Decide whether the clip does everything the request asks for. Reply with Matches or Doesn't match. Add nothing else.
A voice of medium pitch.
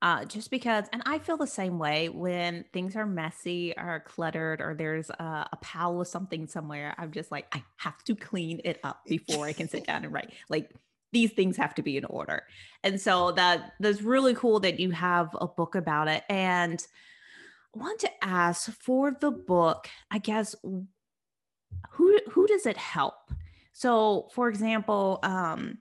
Matches